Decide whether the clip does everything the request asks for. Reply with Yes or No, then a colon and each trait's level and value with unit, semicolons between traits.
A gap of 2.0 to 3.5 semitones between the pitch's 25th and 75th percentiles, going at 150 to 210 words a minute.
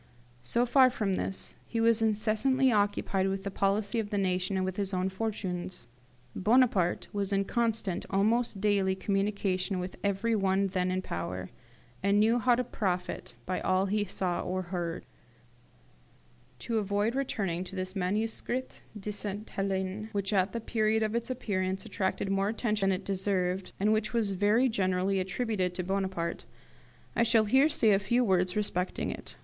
Yes: average, 2.7 semitones; average, 165 wpm